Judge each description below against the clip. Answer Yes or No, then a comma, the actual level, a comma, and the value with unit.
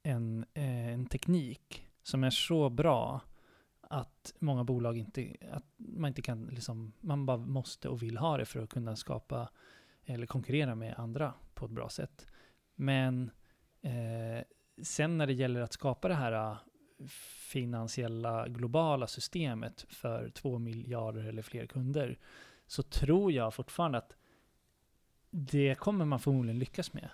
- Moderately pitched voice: No, low, 130 Hz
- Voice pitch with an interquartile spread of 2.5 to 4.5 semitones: Yes, average, 3.9 semitones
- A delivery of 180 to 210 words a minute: No, average, 145 wpm